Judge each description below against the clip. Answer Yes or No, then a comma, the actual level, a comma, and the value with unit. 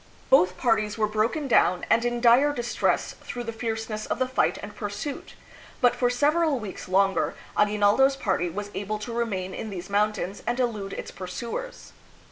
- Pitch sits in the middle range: No, high, 220 Hz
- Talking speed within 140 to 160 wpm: No, average, 180 wpm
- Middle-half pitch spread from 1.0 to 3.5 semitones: Yes, average, 3.2 semitones